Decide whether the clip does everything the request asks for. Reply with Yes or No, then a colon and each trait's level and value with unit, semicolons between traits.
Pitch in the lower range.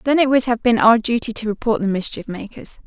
No: high, 230 Hz